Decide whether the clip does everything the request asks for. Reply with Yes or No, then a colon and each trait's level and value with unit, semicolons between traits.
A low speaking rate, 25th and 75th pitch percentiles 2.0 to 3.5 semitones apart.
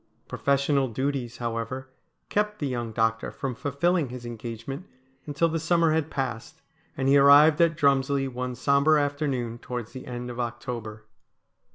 No: average, 155 wpm; average, 3.2 semitones